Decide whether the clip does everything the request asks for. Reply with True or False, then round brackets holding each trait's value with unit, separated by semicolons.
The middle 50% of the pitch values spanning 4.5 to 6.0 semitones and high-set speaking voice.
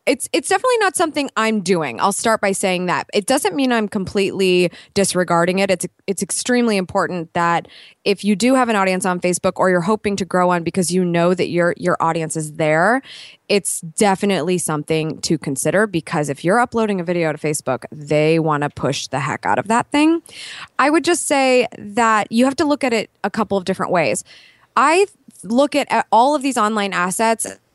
True (4.8 semitones; 195 Hz)